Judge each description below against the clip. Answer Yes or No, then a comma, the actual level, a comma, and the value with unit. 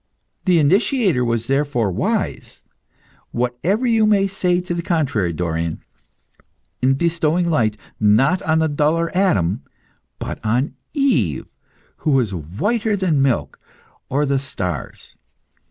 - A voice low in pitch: No, medium, 145 Hz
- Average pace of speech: No, slow, 120 wpm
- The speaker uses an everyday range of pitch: No, wide, 7.7 semitones